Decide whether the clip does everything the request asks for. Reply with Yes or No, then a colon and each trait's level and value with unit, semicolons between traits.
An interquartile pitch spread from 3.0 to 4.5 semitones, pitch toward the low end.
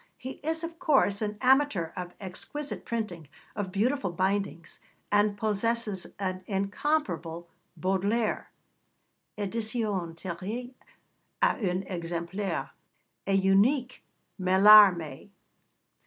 No: average, 4.1 semitones; high, 200 Hz